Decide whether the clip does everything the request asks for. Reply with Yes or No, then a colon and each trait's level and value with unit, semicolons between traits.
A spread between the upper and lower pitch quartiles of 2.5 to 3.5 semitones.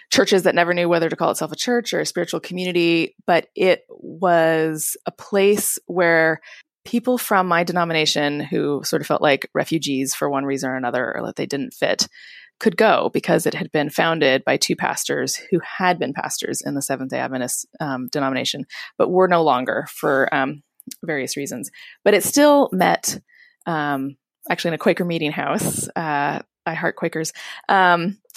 No: average, 4.2 semitones